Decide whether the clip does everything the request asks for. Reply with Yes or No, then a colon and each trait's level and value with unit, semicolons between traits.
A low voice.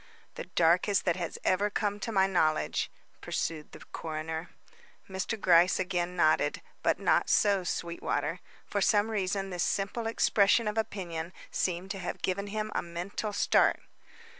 No: high, 190 Hz